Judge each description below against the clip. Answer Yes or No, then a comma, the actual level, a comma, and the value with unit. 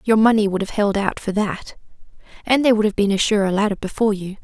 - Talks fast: Yes, fast, 245 wpm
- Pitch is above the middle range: Yes, high, 205 Hz